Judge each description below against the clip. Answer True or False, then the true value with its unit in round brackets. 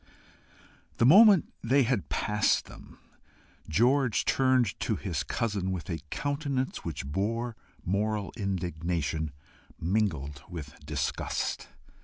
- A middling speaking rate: False (105 wpm)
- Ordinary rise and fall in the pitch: False (7.0 semitones)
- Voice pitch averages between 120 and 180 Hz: False (105 Hz)